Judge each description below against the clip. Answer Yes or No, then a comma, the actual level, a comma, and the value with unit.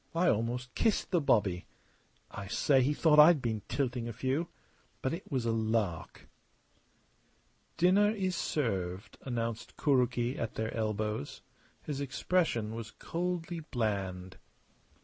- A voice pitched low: Yes, low, 125 Hz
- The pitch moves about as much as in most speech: No, wide, 5.8 semitones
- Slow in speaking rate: Yes, slow, 130 wpm